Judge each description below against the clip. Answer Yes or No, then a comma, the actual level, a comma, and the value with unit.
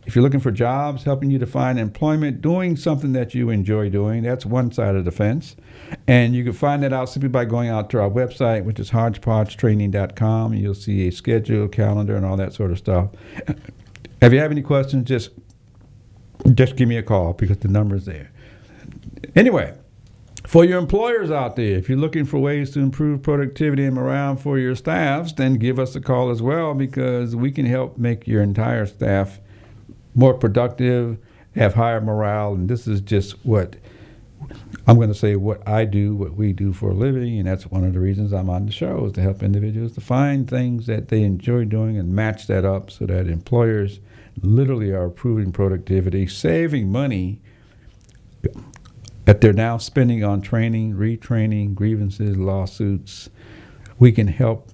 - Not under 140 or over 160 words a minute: No, average, 185 wpm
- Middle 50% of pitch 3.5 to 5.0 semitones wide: Yes, average, 3.8 semitones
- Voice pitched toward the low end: Yes, low, 110 Hz